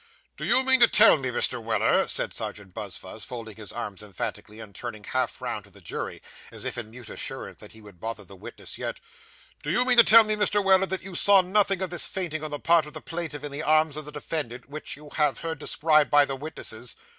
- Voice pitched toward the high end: No, medium, 150 Hz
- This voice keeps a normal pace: No, fast, 240 wpm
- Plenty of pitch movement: Yes, wide, 7.8 semitones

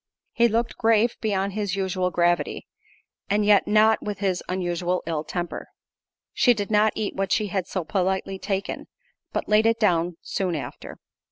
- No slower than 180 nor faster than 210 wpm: No, average, 165 wpm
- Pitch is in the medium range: No, high, 195 Hz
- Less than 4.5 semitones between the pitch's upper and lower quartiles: Yes, average, 2.8 semitones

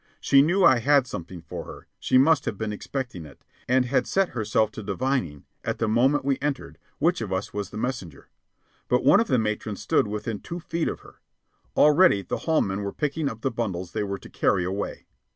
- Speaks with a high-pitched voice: No, low, 115 Hz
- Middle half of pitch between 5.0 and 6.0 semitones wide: Yes, wide, 5.5 semitones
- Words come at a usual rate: No, fast, 215 wpm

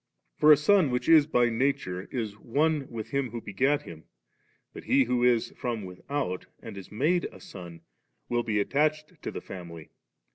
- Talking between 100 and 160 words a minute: No, average, 185 wpm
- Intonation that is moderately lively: No, wide, 6.4 semitones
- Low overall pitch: Yes, low, 125 Hz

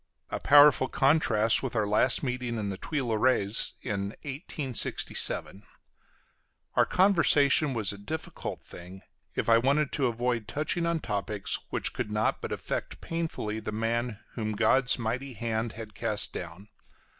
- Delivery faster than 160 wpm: No, average, 145 wpm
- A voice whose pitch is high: No, low, 115 Hz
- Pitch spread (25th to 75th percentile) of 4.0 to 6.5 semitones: Yes, average, 4.4 semitones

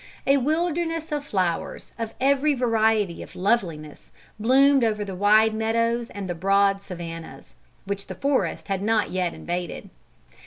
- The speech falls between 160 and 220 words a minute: No, average, 145 wpm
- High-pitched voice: Yes, high, 215 Hz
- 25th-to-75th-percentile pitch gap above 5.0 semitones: Yes, wide, 5.6 semitones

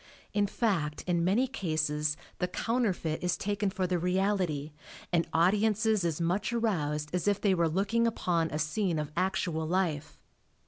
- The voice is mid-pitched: Yes, medium, 180 Hz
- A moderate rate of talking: Yes, average, 155 wpm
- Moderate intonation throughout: Yes, average, 4.3 semitones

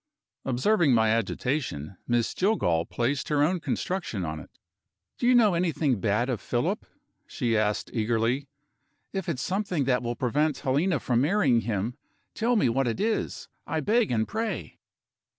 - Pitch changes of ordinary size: No, wide, 7.8 semitones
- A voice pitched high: No, low, 130 Hz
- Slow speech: No, average, 155 wpm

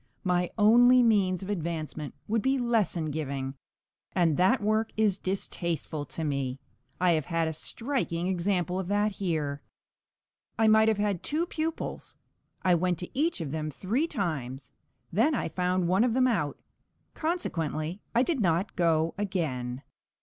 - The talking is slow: No, average, 155 wpm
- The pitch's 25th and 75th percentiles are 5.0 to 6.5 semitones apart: Yes, wide, 5.4 semitones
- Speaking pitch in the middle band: Yes, medium, 180 Hz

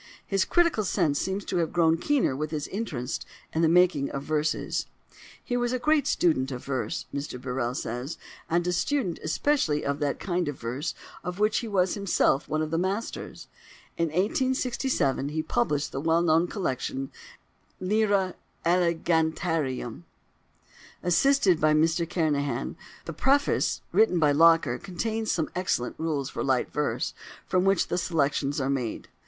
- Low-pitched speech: No, medium, 165 Hz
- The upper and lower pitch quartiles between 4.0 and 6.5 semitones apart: Yes, average, 4.9 semitones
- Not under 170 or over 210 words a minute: No, average, 155 wpm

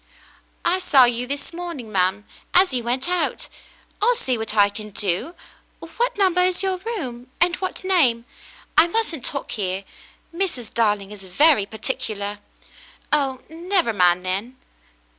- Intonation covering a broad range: Yes, wide, 9.0 semitones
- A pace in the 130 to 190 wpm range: Yes, average, 150 wpm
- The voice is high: Yes, very high, 260 Hz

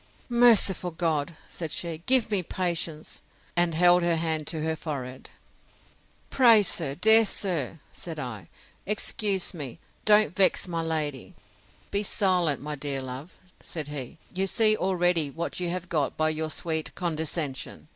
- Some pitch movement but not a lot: Yes, average, 3.5 semitones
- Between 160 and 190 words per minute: No, average, 145 wpm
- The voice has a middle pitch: Yes, medium, 165 Hz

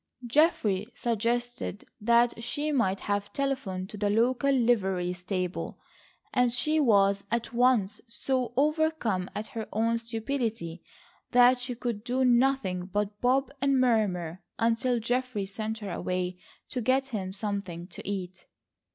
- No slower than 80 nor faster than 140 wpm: Yes, slow, 135 wpm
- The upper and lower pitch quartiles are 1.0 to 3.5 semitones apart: No, average, 4.2 semitones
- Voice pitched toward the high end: Yes, high, 230 Hz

